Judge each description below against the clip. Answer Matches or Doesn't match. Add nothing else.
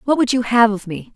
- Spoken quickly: Matches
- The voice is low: Doesn't match